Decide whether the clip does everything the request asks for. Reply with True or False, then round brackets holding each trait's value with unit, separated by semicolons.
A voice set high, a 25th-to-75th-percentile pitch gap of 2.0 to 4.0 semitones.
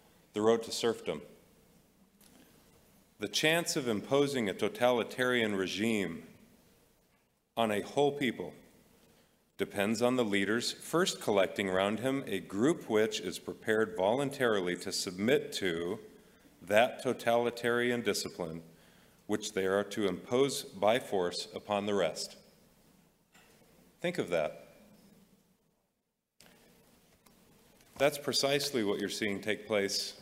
False (110 Hz; 3.7 semitones)